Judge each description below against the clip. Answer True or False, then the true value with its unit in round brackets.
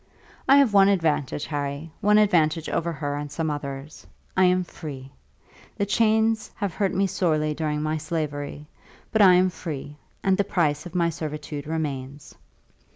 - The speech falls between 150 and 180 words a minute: True (160 wpm)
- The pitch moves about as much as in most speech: True (4.2 semitones)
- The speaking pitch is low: False (160 Hz)